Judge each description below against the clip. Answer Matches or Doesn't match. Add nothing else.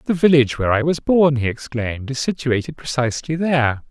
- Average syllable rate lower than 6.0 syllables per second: Doesn't match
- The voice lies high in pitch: Doesn't match